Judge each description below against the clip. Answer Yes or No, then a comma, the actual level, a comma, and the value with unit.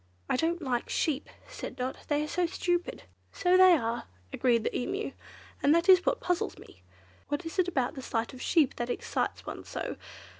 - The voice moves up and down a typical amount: No, wide, 5.8 semitones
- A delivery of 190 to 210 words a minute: Yes, average, 195 wpm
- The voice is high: Yes, very high, 305 Hz